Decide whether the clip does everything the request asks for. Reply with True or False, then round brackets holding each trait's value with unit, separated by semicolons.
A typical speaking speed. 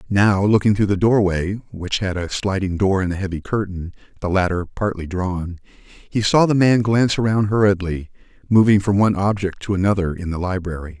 True (185 wpm)